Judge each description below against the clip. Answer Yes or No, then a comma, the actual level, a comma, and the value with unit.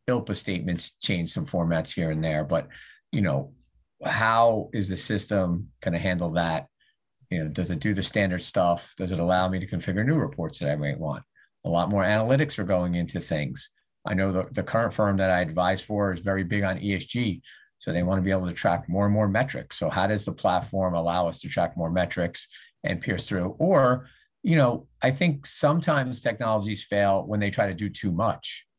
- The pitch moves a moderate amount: Yes, average, 3.7 semitones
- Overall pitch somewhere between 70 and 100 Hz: Yes, very low, 95 Hz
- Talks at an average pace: No, fast, 215 wpm